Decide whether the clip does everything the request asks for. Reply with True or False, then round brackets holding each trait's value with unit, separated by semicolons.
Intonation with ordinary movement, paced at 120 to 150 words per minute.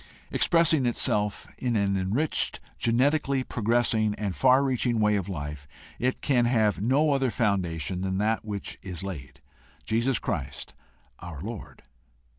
True (4.9 semitones; 135 wpm)